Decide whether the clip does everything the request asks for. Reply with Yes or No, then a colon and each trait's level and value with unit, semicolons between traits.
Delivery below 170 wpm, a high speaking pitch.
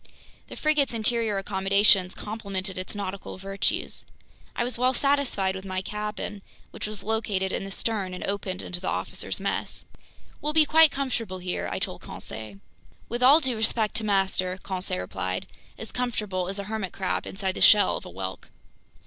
No: average, 175 wpm; high, 200 Hz